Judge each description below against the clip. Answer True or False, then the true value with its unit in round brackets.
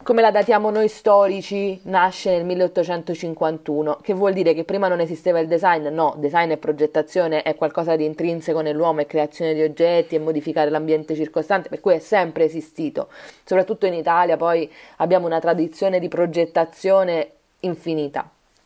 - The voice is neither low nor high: True (170 Hz)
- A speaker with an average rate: True (160 wpm)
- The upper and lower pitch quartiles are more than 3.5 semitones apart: False (2.8 semitones)